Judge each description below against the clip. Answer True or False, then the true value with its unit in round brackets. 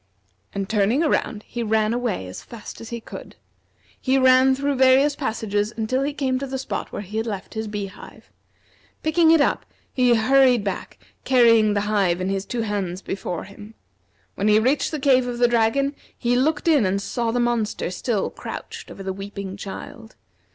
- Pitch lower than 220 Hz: False (230 Hz)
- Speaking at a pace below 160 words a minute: False (190 wpm)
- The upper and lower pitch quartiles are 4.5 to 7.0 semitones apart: False (4.1 semitones)